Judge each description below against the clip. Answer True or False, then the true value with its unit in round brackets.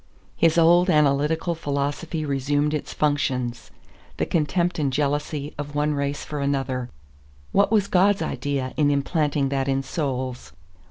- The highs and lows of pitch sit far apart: False (2.4 semitones)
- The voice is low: False (145 Hz)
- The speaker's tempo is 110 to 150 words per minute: True (140 wpm)